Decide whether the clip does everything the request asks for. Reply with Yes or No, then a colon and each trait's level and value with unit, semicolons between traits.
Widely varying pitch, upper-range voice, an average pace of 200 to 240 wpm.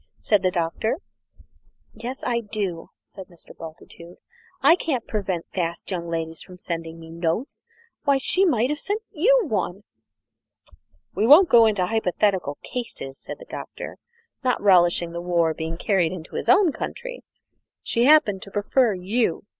No: wide, 6.6 semitones; high, 200 Hz; average, 155 wpm